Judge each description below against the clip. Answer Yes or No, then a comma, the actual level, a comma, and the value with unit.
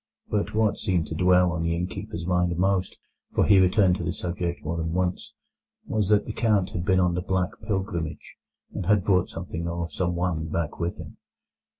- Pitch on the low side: Yes, very low, 90 Hz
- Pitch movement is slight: Yes, narrow, 1.8 semitones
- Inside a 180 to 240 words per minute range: Yes, average, 185 wpm